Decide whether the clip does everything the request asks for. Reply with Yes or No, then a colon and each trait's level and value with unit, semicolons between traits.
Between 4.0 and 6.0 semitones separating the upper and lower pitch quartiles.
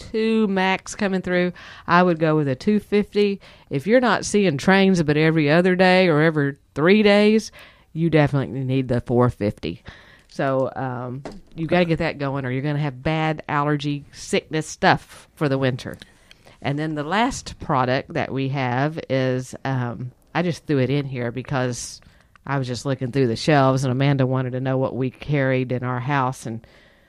Yes: average, 4.5 semitones